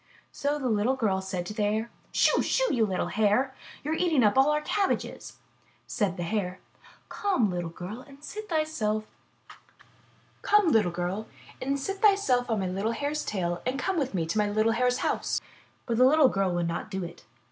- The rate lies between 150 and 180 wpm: Yes, average, 170 wpm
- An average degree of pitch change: No, wide, 6.7 semitones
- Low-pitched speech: No, high, 225 Hz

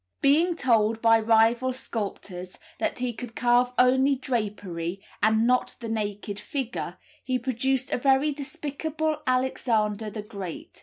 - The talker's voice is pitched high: Yes, high, 240 Hz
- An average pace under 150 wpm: Yes, slow, 135 wpm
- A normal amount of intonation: Yes, average, 3.7 semitones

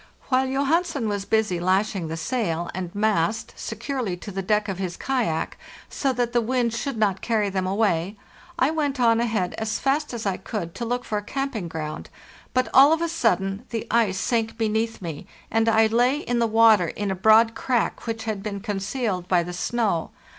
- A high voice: Yes, high, 220 Hz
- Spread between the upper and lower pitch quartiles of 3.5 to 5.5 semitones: Yes, average, 3.9 semitones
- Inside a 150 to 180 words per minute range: No, average, 195 wpm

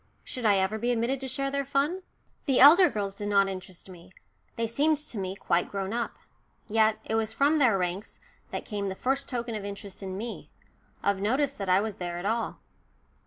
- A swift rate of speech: Yes, fast, 210 wpm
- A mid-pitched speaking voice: No, high, 220 Hz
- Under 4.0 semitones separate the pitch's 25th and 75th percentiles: No, average, 5.1 semitones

